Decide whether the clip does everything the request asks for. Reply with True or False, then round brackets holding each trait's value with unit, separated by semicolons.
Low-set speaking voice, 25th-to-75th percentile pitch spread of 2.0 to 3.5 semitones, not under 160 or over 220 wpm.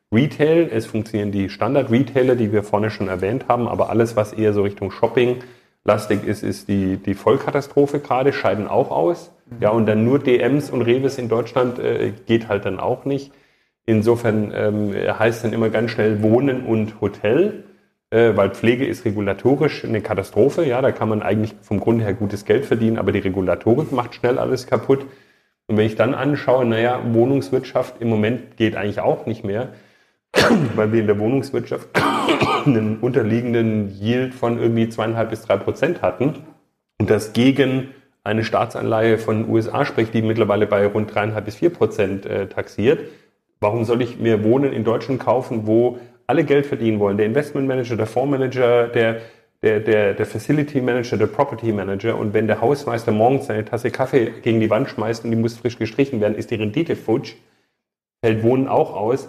True (115 Hz; 2.8 semitones; 180 wpm)